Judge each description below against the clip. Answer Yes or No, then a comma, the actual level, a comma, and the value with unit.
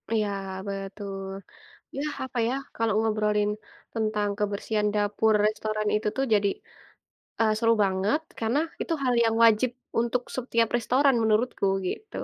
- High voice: Yes, high, 215 Hz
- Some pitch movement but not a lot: No, narrow, 2.1 semitones